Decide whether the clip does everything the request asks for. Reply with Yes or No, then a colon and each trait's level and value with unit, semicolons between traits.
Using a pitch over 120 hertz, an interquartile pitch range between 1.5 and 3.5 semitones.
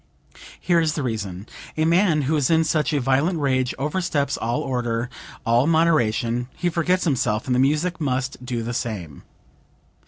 No: low, 135 Hz; average, 5.0 semitones